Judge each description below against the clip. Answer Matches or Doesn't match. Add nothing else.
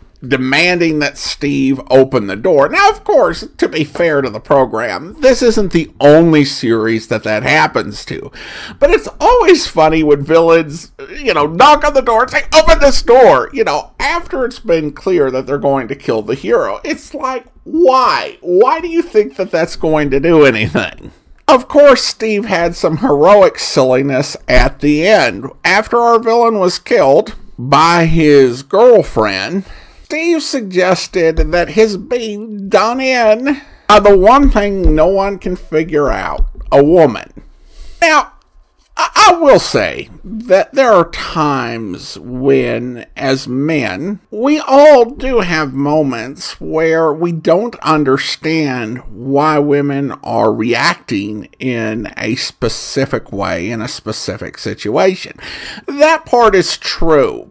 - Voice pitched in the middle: Matches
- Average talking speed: Matches